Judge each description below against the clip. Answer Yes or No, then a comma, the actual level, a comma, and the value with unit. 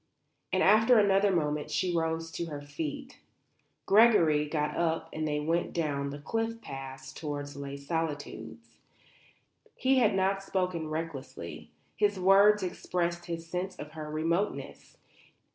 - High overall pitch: No, medium, 165 Hz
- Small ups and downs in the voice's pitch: No, average, 4.5 semitones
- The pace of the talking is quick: No, slow, 135 wpm